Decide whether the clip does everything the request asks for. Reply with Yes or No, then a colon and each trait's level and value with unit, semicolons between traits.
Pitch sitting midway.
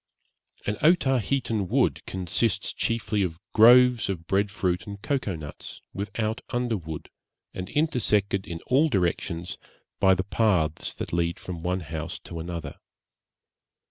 No: very low, 95 Hz